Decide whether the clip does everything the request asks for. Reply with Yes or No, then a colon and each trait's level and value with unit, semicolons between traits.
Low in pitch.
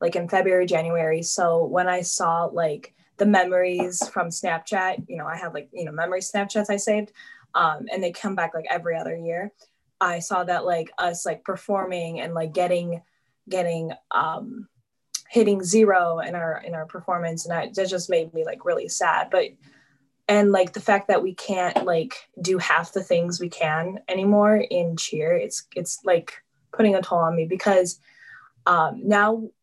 No: medium, 180 Hz